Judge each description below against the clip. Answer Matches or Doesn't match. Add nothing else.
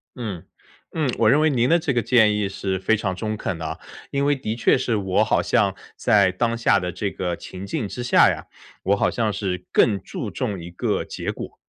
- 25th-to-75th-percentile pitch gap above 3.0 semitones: Matches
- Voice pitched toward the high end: Doesn't match